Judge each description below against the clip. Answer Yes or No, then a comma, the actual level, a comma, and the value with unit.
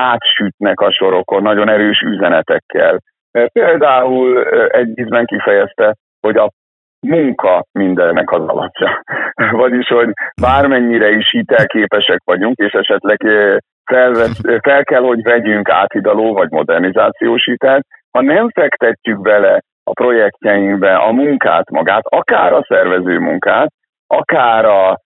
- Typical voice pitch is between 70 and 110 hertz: No, low, 120 Hz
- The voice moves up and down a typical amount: Yes, average, 3.3 semitones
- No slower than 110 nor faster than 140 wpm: Yes, average, 115 wpm